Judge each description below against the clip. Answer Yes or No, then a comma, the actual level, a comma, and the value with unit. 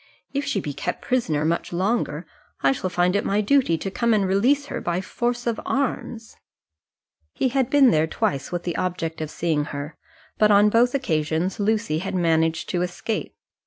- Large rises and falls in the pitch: Yes, wide, 6.3 semitones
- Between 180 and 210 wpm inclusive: Yes, average, 190 wpm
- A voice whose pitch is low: No, medium, 185 Hz